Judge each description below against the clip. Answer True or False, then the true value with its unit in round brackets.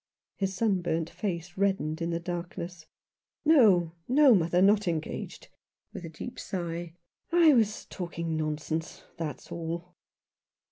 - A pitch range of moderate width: True (3.3 semitones)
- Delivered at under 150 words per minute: True (140 wpm)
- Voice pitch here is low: False (175 Hz)